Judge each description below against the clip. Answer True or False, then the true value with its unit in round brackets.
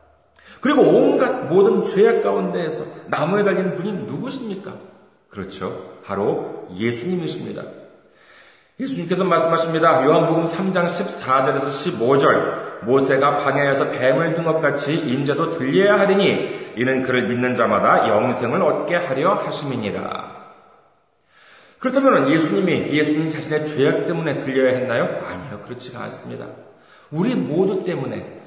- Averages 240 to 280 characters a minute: False (305 characters per minute)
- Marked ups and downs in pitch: True (6.6 semitones)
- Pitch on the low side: False (165 Hz)